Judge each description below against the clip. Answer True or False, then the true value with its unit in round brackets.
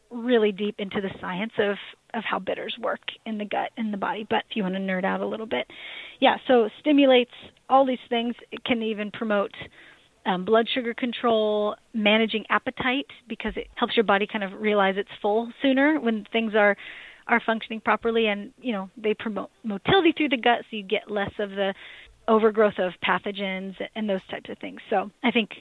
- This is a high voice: True (220 Hz)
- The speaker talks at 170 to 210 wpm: True (200 wpm)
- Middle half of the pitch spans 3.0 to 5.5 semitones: False (2.6 semitones)